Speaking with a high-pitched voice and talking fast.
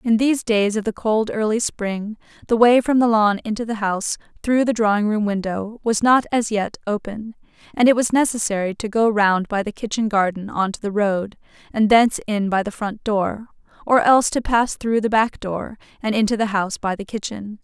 Yes: high, 215 Hz; fast, 215 wpm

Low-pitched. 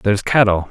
Yes: low, 105 Hz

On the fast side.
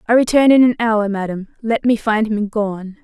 Yes: fast, 220 wpm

